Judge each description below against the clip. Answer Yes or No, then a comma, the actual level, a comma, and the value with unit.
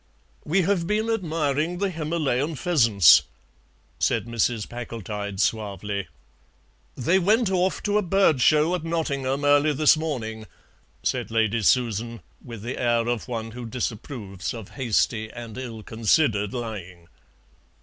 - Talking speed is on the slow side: Yes, slow, 130 wpm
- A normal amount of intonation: No, wide, 6.3 semitones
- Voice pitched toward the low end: Yes, low, 125 Hz